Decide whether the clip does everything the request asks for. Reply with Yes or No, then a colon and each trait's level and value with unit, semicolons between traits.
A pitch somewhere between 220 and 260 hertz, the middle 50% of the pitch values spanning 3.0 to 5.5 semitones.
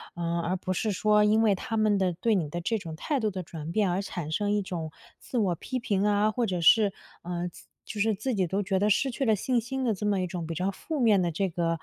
No: high, 195 Hz; average, 3.6 semitones